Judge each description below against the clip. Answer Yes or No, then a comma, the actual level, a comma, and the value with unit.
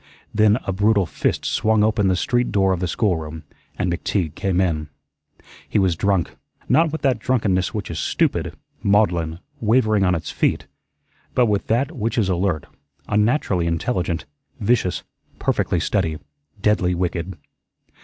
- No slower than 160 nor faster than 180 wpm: No, average, 145 wpm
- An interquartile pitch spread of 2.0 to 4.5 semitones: Yes, average, 3.8 semitones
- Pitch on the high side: No, very low, 95 Hz